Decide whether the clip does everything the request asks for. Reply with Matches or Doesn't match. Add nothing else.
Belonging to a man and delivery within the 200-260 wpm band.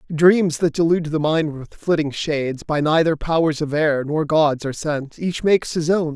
Matches